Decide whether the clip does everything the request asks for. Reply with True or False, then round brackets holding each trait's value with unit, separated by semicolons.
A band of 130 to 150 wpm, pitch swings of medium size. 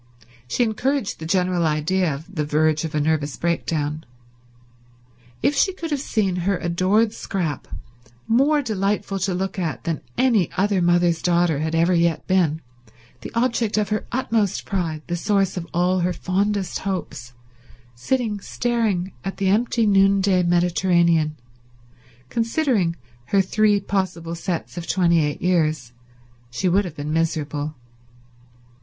True (140 wpm; 3.8 semitones)